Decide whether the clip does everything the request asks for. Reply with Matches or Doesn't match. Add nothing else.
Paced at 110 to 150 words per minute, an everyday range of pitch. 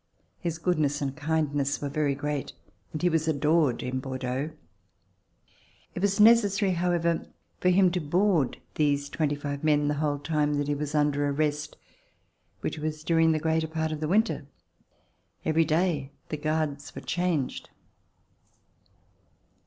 Doesn't match